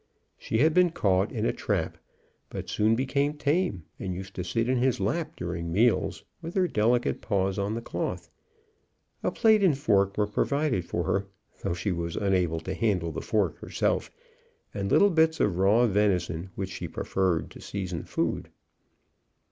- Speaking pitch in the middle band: No, low, 105 Hz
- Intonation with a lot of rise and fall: Yes, wide, 6.2 semitones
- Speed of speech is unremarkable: Yes, average, 170 wpm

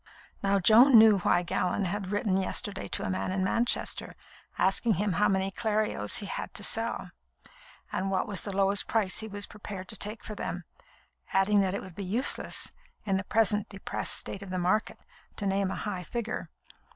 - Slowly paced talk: No, average, 190 wpm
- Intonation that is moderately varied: No, narrow, 2.0 semitones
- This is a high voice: Yes, high, 200 Hz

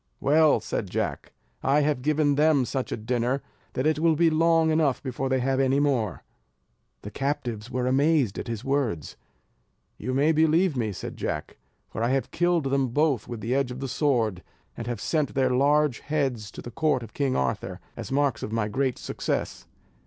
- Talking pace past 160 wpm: Yes, average, 190 wpm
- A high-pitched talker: No, low, 135 Hz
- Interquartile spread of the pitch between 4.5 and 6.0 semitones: No, average, 3.6 semitones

